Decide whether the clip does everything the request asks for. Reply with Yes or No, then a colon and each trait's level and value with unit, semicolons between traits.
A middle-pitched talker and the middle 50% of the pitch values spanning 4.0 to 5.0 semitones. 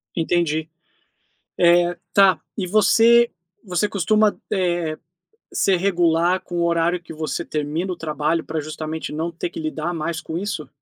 No: medium, 175 Hz; average, 2.8 semitones